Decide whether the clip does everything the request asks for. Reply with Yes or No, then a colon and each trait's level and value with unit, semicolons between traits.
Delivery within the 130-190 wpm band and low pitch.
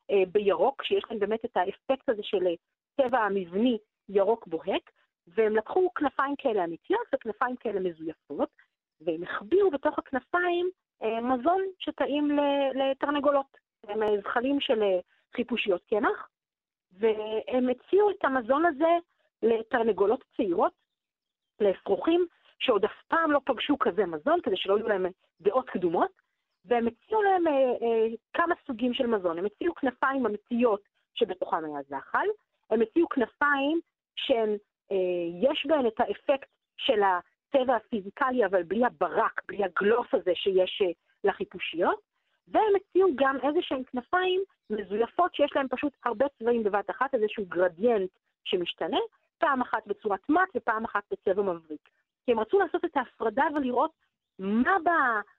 No: average, 135 wpm; very high, 250 Hz